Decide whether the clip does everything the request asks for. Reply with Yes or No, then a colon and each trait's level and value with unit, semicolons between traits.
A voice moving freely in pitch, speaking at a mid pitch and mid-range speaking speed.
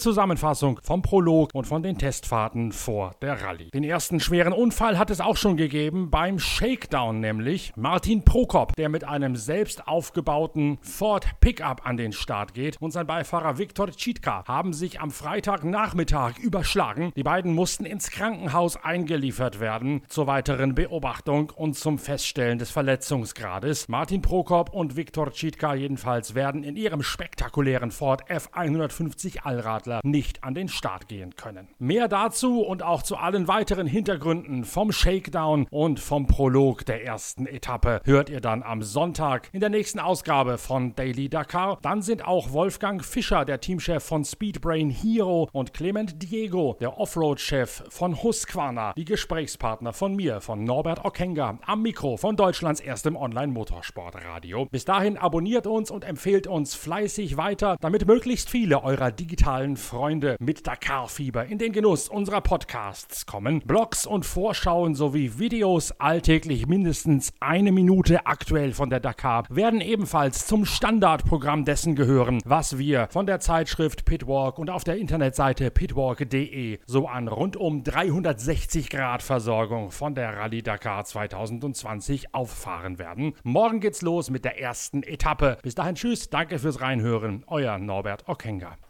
Yes: wide, 5.7 semitones; medium, 150 Hz; average, 150 wpm